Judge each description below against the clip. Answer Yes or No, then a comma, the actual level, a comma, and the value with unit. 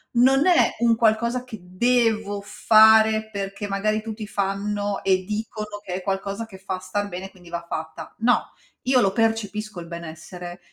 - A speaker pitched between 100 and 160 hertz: No, high, 205 Hz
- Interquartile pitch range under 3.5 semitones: Yes, average, 2.7 semitones